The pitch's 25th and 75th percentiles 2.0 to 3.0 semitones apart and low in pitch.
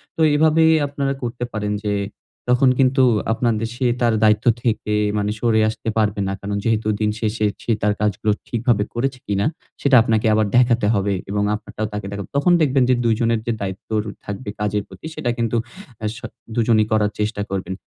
Yes: average, 2.7 semitones; low, 110 Hz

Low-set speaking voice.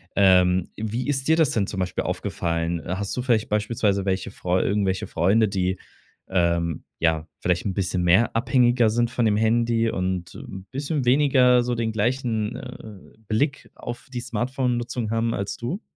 Yes: low, 110 Hz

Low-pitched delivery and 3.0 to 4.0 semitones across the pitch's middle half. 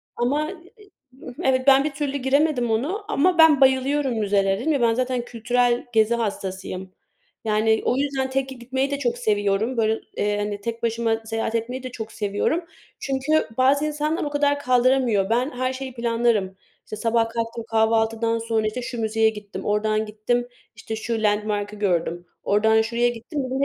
No: high, 235 Hz; average, 3.4 semitones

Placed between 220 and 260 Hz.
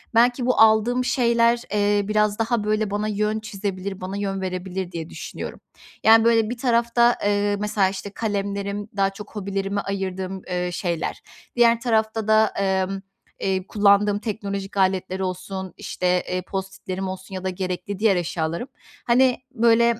No: high, 200 Hz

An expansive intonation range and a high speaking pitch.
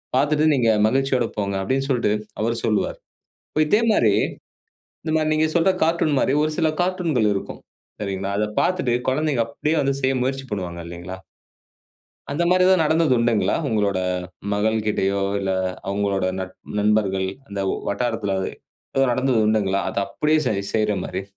No: wide, 7.0 semitones; low, 115 Hz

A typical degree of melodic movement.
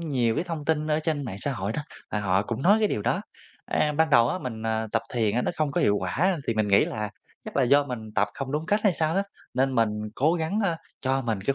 No: wide, 6.0 semitones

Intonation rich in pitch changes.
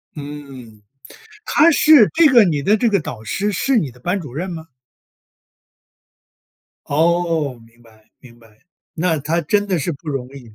Yes: wide, 7.1 semitones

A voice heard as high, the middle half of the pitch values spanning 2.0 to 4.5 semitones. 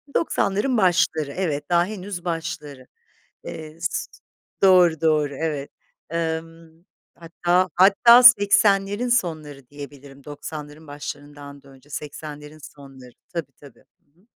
No: medium, 160 Hz; average, 3.9 semitones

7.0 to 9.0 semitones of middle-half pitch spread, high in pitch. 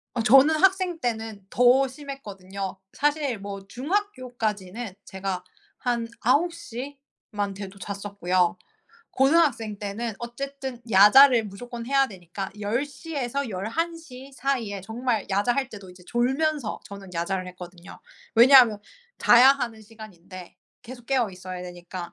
No: wide, 5.4 semitones; high, 230 Hz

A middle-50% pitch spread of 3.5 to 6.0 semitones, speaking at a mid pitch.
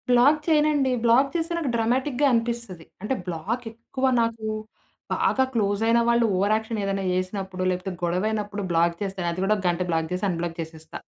No: average, 4.6 semitones; high, 210 Hz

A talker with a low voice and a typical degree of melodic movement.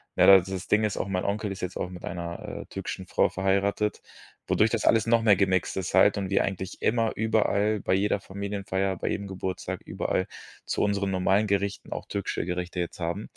No: very low, 95 Hz; narrow, 1.8 semitones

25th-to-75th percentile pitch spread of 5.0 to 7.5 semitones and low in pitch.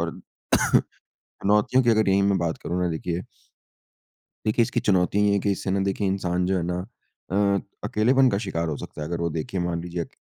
No: average, 2.9 semitones; very low, 95 Hz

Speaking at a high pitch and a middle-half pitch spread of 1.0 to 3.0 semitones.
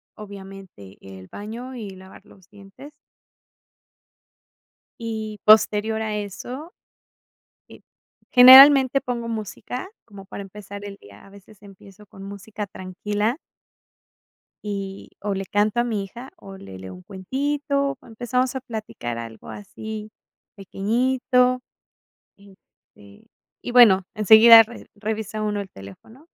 No: high, 210 Hz; average, 3.5 semitones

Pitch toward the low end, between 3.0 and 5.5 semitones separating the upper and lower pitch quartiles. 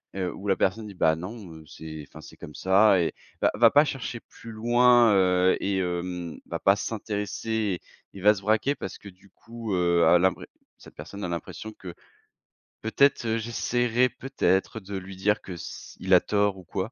Yes: low, 100 Hz; average, 3.6 semitones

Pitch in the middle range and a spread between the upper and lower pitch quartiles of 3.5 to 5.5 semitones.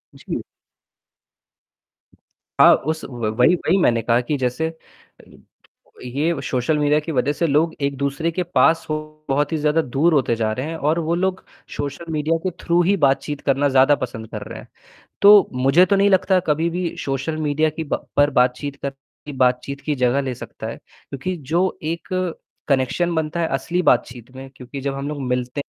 Yes: medium, 145 Hz; average, 3.9 semitones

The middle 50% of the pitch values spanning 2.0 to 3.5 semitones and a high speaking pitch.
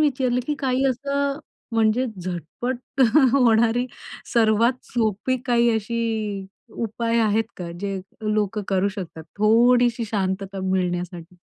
No: average, 4.1 semitones; high, 225 Hz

